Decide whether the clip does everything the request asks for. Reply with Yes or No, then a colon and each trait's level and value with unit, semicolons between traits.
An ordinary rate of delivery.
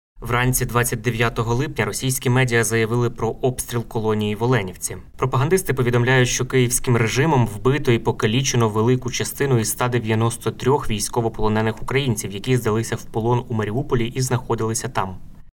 Yes: average, 130 wpm